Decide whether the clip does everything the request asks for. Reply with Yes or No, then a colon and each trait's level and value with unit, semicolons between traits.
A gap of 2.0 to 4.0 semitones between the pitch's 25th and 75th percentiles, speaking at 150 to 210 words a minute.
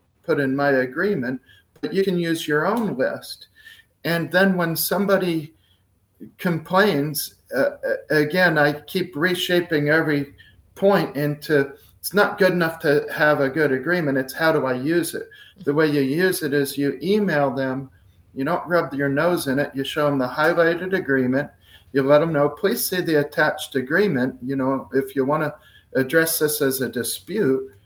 No: average, 4.7 semitones; average, 175 wpm